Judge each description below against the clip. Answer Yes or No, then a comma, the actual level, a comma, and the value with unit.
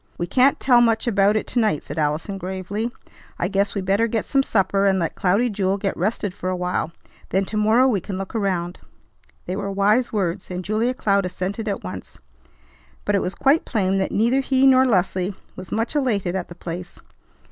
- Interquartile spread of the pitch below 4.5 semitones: Yes, average, 3.4 semitones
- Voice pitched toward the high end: Yes, high, 200 Hz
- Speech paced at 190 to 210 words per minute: Yes, fast, 205 wpm